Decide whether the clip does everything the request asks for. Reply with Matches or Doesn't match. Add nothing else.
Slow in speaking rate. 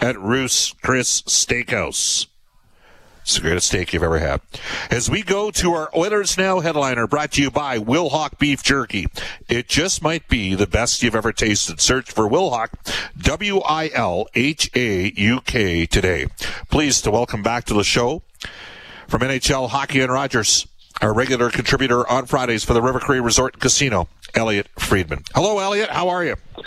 Doesn't match